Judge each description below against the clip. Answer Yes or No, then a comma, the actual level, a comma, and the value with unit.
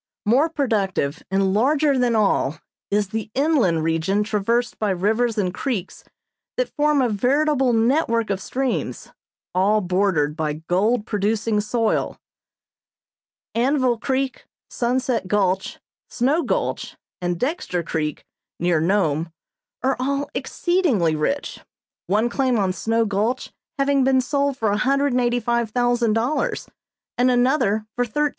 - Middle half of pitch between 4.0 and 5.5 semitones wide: Yes, average, 5.1 semitones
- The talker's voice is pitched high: Yes, high, 230 Hz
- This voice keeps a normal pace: No, slow, 120 wpm